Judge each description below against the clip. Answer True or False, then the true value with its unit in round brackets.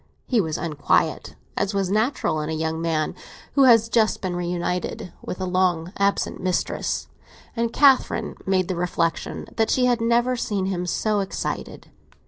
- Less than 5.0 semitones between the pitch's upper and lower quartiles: True (4.6 semitones)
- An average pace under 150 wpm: False (160 wpm)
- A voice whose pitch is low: False (190 Hz)